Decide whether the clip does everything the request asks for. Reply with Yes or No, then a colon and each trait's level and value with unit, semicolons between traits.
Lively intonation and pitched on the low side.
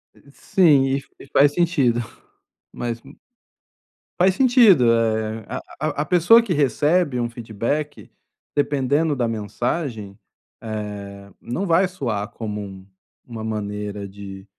Yes: wide, 6.4 semitones; low, 120 Hz